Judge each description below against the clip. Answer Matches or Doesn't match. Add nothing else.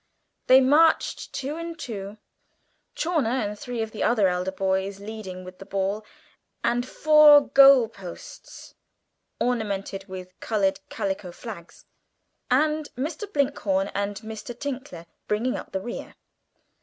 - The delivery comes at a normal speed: Doesn't match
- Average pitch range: Doesn't match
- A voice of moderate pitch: Doesn't match